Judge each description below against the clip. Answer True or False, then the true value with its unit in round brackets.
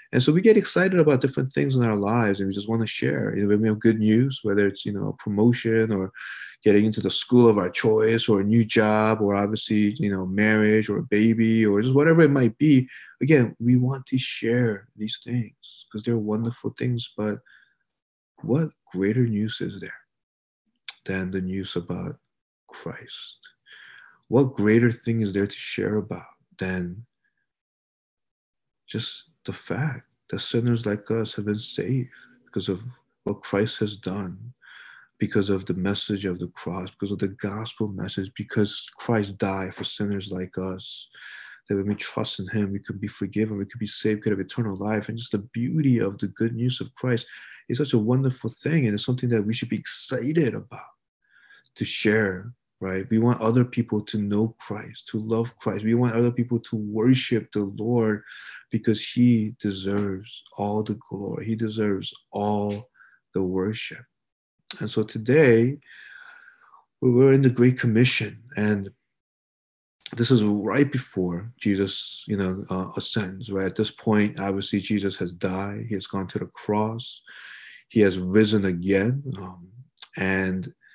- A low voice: True (110 Hz)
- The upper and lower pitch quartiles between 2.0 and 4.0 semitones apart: True (3.1 semitones)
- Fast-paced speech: False (175 wpm)